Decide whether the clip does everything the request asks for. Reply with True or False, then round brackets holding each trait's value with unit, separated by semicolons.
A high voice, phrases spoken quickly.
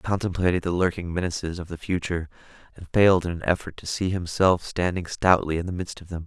False (90 Hz; 220 wpm)